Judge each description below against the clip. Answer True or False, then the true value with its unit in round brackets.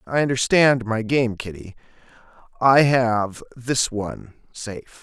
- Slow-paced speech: True (120 wpm)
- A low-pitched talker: True (120 Hz)